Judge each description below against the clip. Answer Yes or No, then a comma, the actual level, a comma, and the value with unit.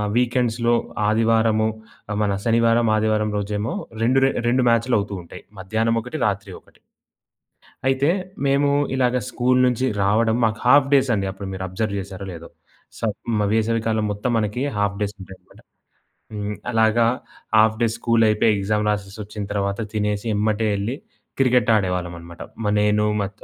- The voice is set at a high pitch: No, low, 110 Hz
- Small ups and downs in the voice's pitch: Yes, narrow, 2.3 semitones